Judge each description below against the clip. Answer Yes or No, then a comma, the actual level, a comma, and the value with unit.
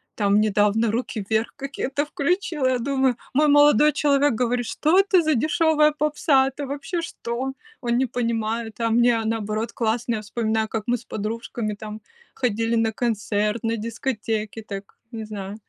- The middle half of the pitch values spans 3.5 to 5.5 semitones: Yes, average, 4.1 semitones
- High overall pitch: Yes, high, 235 Hz